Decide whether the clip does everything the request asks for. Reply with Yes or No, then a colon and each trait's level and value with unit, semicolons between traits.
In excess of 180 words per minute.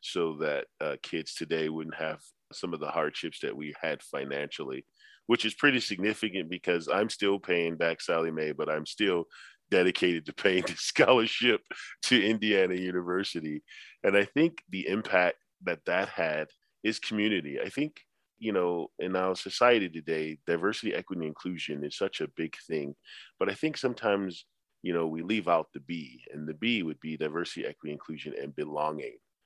No: average, 170 wpm